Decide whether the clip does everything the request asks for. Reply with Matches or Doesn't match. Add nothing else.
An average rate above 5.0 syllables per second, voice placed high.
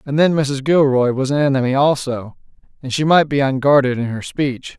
Doesn't match